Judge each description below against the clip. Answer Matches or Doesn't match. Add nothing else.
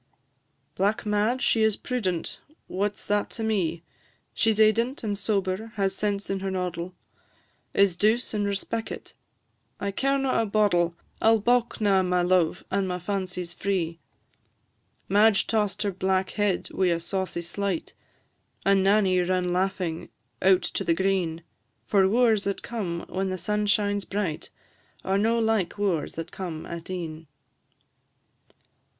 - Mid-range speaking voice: Doesn't match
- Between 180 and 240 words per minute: Doesn't match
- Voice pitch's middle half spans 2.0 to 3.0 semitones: Matches